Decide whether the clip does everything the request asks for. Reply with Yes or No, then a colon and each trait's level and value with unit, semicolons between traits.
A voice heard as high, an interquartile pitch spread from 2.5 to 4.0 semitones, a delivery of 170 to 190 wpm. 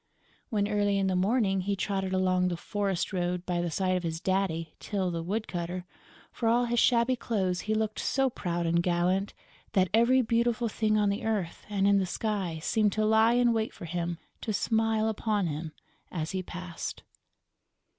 Yes: high, 195 Hz; average, 3.6 semitones; average, 185 wpm